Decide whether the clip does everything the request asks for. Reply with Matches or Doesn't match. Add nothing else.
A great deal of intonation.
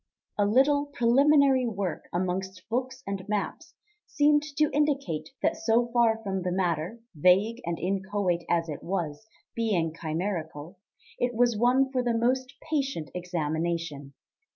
Matches